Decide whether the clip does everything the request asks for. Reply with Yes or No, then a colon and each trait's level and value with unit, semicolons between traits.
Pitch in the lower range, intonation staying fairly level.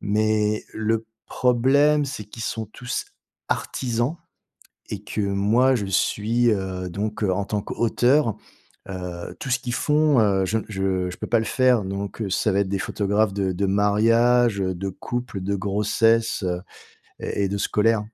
No: low, 105 Hz; average, 3.2 semitones